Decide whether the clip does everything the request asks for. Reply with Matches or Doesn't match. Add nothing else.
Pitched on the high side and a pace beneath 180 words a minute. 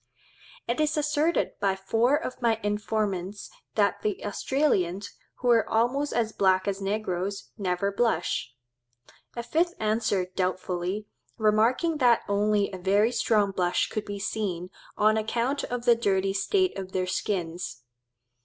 Matches